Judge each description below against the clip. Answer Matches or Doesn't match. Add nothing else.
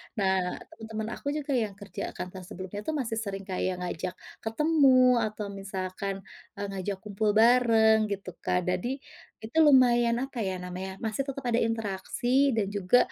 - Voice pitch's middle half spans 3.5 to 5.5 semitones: Matches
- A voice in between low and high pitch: Doesn't match